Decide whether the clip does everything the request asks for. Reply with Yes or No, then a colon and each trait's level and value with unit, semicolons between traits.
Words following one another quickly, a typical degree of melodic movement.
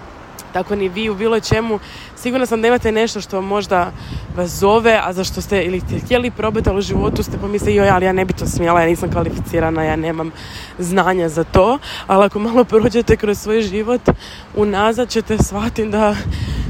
Yes: fast, 190 wpm; average, 3.3 semitones